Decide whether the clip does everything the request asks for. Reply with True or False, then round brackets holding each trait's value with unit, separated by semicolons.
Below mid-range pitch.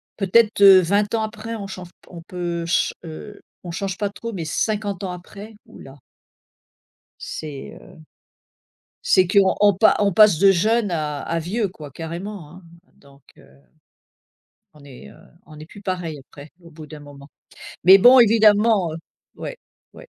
False (185 Hz)